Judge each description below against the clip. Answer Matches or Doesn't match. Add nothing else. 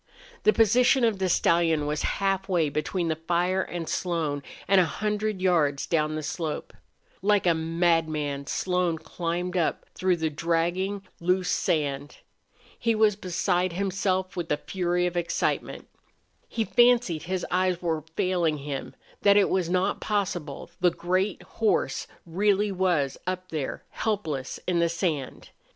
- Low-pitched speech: Doesn't match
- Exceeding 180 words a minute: Doesn't match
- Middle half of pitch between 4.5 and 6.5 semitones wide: Doesn't match